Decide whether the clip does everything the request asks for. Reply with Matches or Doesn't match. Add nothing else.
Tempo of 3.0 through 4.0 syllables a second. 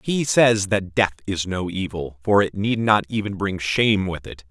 Doesn't match